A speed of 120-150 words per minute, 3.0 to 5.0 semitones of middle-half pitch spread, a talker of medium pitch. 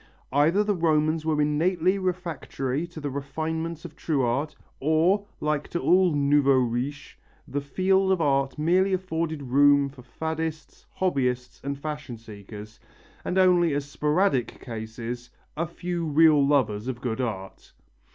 Yes: average, 140 wpm; average, 3.9 semitones; medium, 150 Hz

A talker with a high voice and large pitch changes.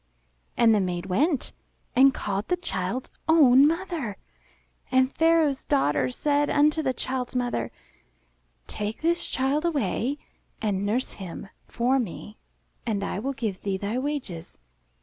Yes: very high, 250 Hz; wide, 6.3 semitones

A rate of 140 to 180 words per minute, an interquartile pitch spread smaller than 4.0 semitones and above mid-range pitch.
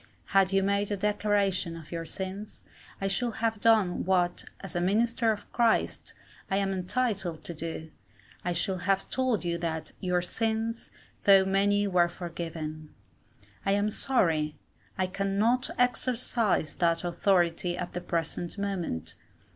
Yes: average, 145 wpm; average, 3.3 semitones; high, 195 Hz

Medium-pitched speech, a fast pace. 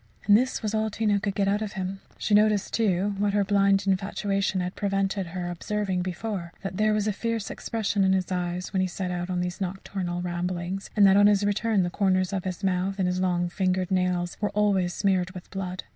No: high, 195 Hz; fast, 220 wpm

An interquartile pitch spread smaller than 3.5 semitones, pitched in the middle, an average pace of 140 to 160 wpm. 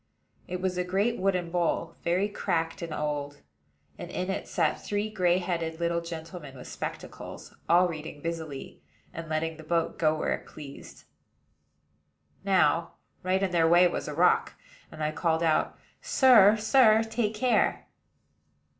Yes: average, 2.9 semitones; medium, 170 Hz; average, 155 wpm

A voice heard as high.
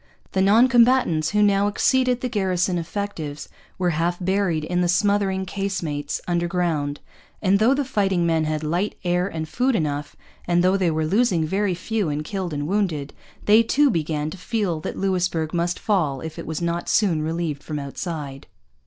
No: medium, 180 Hz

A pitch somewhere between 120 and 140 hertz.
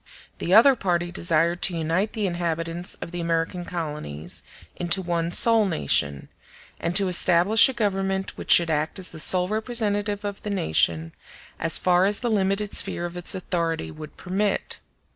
No: medium, 175 Hz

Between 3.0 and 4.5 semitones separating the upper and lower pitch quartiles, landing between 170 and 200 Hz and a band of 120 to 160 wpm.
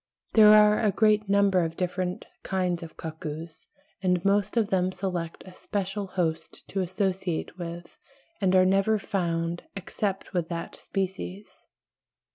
No: narrow, 2.4 semitones; medium, 185 Hz; average, 140 wpm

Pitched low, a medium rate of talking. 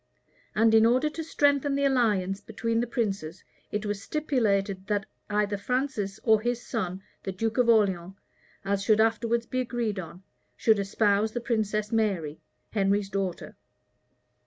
No: high, 215 Hz; average, 150 wpm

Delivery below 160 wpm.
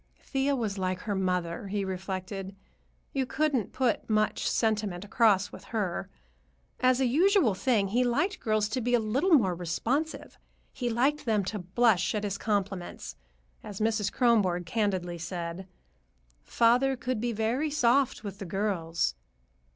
Yes: average, 150 wpm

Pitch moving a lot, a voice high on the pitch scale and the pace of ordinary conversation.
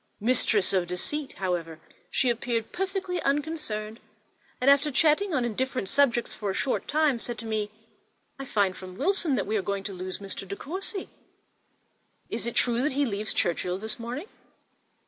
Yes: wide, 6.1 semitones; high, 235 Hz; average, 165 wpm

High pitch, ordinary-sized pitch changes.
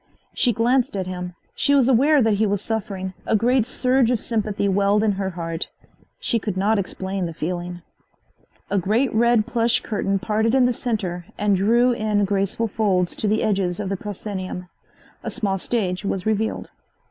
Yes: high, 205 Hz; average, 3.2 semitones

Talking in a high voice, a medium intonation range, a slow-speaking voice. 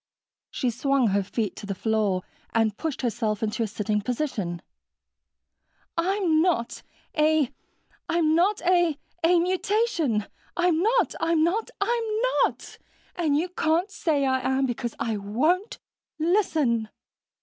No: very high, 305 Hz; wide, 7.6 semitones; slow, 120 wpm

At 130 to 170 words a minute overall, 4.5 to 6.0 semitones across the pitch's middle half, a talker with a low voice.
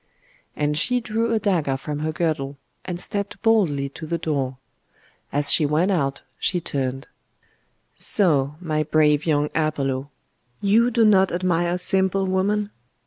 No: average, 140 wpm; average, 4.8 semitones; medium, 165 Hz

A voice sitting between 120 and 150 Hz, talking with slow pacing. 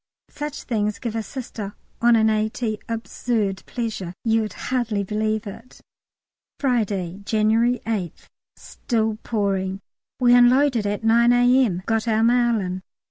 No: high, 220 Hz; slow, 130 wpm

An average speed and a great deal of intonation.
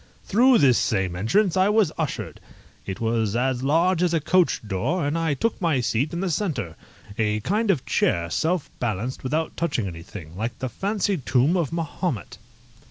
Yes: average, 175 wpm; wide, 8.0 semitones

